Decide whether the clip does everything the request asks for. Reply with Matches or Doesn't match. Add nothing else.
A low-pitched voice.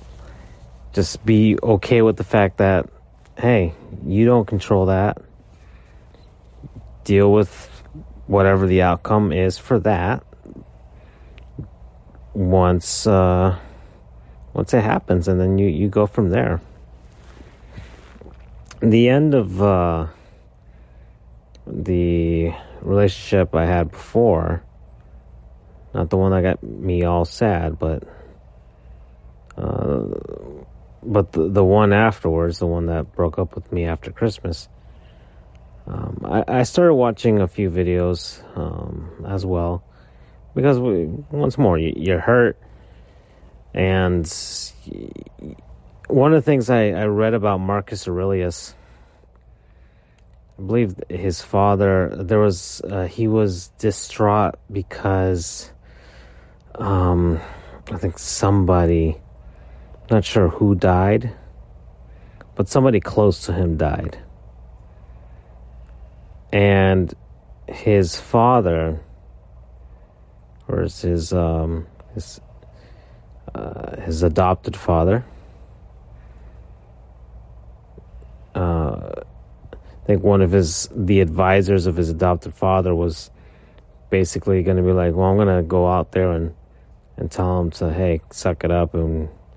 Matches